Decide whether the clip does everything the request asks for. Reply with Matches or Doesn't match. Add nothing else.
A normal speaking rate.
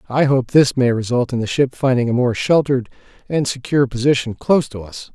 Doesn't match